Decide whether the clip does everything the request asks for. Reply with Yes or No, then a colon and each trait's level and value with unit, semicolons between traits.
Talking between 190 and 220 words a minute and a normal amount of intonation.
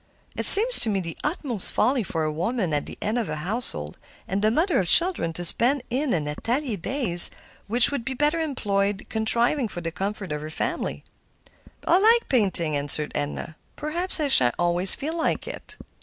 No: average, 195 wpm; wide, 8.6 semitones